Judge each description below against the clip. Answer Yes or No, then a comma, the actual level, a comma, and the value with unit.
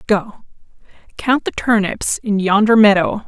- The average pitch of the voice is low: No, high, 210 Hz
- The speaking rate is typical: No, slow, 130 wpm